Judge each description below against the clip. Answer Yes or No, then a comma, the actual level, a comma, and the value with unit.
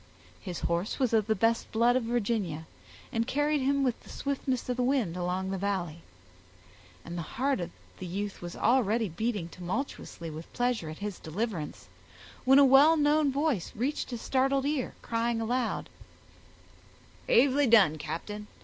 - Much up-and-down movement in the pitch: Yes, wide, 6.4 semitones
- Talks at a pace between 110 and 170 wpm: Yes, average, 160 wpm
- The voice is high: Yes, high, 230 Hz